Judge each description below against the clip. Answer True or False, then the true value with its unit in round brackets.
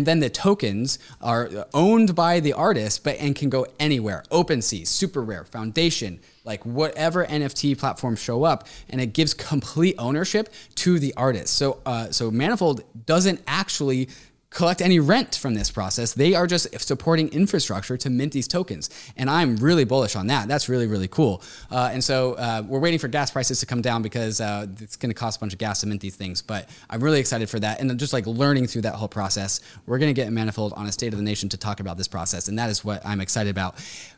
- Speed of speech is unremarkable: False (225 wpm)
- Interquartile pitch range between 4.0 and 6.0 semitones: True (5.6 semitones)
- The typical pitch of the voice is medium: False (125 Hz)